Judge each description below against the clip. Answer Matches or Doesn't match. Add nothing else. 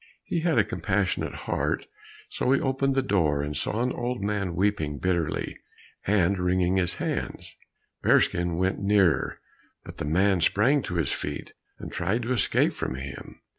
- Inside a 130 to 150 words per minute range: Doesn't match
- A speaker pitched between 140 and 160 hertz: Doesn't match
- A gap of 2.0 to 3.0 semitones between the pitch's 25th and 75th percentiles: Doesn't match